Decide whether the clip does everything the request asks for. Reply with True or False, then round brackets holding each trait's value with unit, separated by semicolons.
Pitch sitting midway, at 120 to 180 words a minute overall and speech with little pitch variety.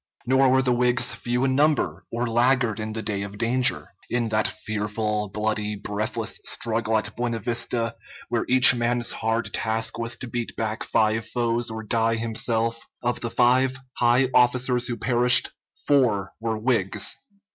False (115 Hz; 160 wpm; 1.9 semitones)